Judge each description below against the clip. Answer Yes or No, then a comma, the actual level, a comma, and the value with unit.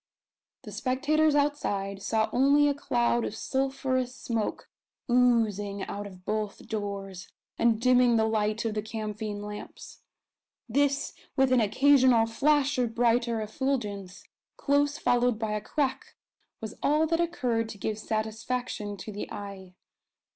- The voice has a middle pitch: No, high, 230 Hz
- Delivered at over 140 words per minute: No, slow, 135 wpm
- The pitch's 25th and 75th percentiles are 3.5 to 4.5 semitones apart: Yes, average, 4.0 semitones